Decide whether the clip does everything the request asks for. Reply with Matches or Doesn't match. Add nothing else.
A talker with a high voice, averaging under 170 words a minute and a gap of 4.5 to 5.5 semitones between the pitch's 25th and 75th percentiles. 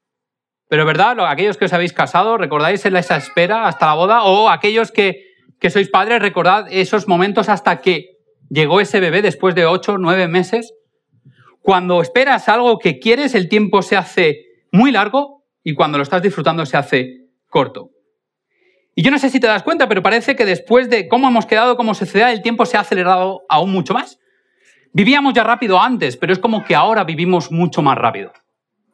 Doesn't match